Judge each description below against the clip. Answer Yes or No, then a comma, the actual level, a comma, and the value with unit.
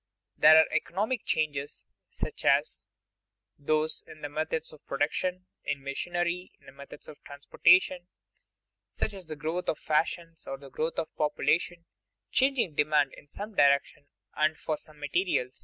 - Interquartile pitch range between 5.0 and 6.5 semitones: No, average, 3.3 semitones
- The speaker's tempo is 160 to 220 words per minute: No, average, 140 wpm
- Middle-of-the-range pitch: Yes, medium, 155 Hz